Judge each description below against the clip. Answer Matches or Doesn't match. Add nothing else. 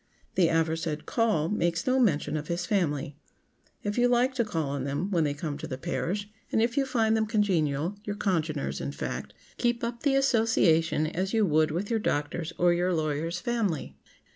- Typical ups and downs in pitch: Doesn't match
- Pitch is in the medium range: Matches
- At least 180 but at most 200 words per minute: Matches